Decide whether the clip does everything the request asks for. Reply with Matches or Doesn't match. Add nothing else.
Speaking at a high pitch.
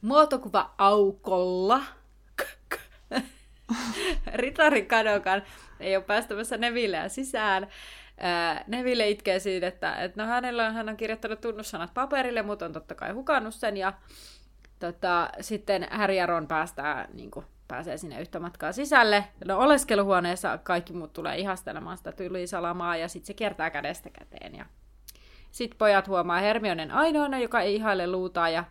Matches